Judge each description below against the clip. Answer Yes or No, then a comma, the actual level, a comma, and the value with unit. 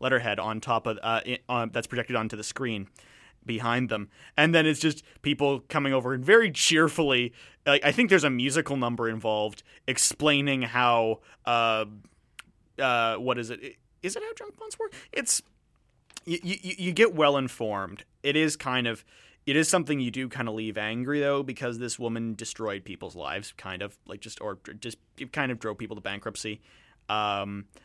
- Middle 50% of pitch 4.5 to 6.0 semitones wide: Yes, average, 4.8 semitones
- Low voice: Yes, low, 125 Hz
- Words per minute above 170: Yes, average, 180 wpm